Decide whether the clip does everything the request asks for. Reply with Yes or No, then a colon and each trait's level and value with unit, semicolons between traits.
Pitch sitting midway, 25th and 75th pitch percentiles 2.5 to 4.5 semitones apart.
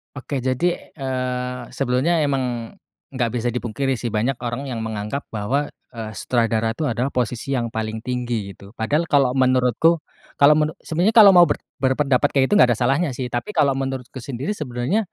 No: low, 130 Hz; average, 3.0 semitones